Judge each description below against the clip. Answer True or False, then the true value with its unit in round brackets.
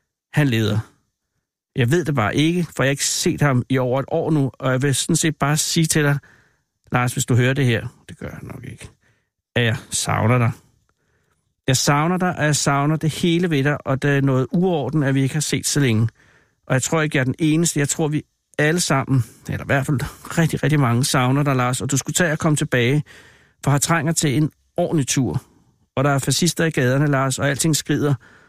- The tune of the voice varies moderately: True (3.1 semitones)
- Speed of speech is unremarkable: False (235 wpm)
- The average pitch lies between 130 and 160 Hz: True (140 Hz)